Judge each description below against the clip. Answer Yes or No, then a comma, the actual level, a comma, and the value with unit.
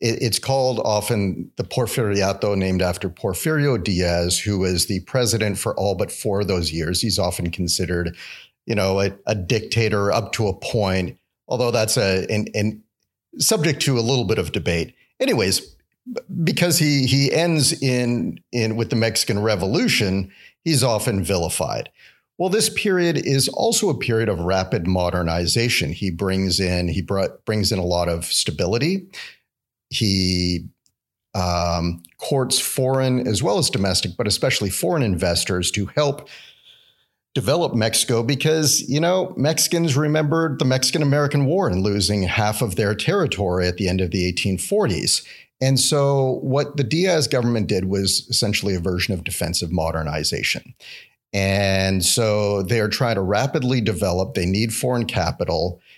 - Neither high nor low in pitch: No, low, 105 Hz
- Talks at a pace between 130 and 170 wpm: Yes, average, 150 wpm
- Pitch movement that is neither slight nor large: No, wide, 5.9 semitones